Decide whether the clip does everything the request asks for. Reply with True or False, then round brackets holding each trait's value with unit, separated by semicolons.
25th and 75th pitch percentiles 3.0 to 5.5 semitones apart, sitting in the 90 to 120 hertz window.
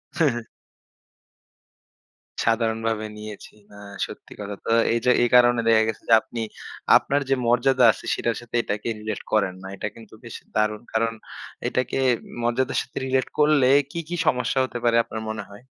False (2.6 semitones; 115 Hz)